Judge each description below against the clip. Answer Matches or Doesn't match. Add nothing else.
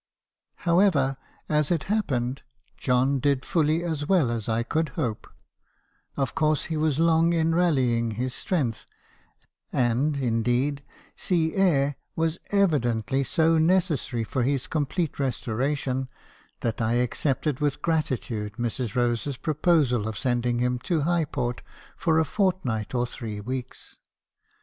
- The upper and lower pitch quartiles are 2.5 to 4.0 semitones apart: Doesn't match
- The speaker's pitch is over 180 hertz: Doesn't match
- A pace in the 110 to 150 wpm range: Matches